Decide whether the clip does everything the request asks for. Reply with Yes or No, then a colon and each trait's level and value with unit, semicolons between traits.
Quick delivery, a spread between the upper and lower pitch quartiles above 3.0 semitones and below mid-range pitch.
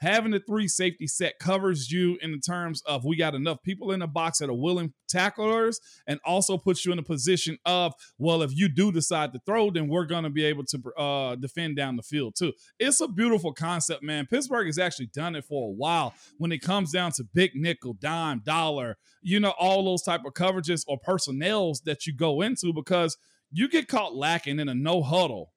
No: fast, 220 wpm; average, 3.5 semitones; medium, 170 Hz